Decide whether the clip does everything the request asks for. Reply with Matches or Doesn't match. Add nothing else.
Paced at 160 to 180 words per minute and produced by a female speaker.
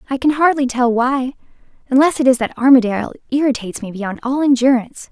Matches